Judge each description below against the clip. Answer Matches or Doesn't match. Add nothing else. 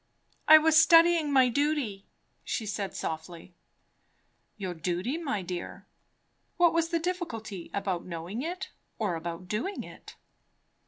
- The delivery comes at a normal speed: Doesn't match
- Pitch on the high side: Matches